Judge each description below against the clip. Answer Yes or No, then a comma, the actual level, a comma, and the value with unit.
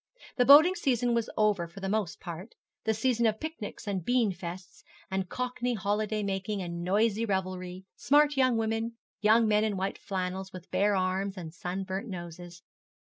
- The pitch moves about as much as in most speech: Yes, average, 3.6 semitones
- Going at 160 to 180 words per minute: Yes, average, 165 wpm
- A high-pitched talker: Yes, high, 205 Hz